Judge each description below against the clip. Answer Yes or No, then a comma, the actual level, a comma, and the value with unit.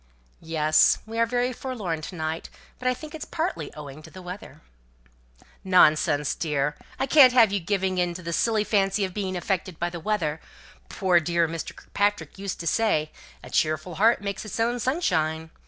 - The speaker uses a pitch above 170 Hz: Yes, medium, 185 Hz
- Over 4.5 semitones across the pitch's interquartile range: Yes, wide, 5.4 semitones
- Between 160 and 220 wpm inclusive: Yes, average, 180 wpm